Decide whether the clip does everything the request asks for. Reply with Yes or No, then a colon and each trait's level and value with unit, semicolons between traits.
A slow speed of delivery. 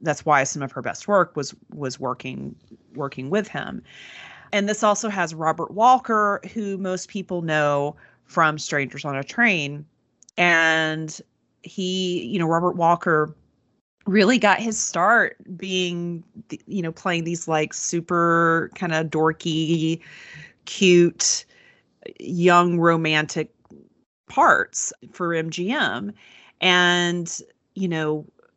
Yes: slow, 120 wpm